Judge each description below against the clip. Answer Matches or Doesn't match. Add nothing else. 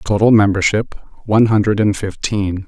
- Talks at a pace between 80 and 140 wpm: Matches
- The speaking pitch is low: Matches